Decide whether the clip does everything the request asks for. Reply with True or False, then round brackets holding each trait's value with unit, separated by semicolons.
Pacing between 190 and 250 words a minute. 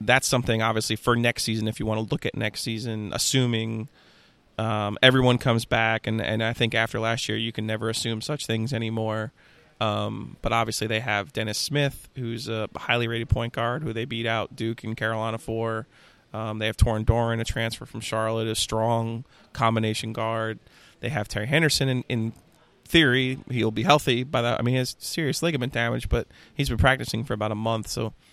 True (200 wpm)